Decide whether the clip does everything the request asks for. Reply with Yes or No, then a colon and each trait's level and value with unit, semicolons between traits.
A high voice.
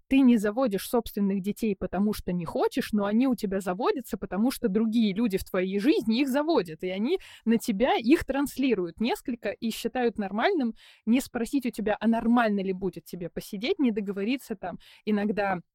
Yes: high, 225 Hz